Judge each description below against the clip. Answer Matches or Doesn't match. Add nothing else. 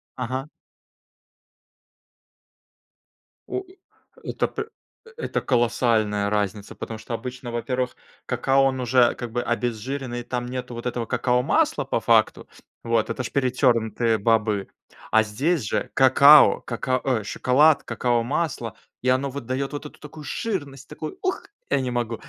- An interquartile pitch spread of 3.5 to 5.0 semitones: Doesn't match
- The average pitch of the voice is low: Matches